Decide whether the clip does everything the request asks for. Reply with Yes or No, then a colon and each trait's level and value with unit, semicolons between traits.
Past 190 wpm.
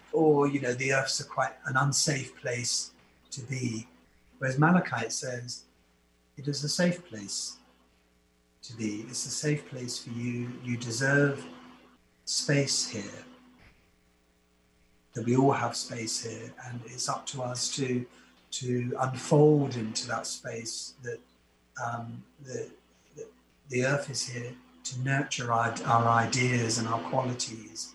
No: average, 140 wpm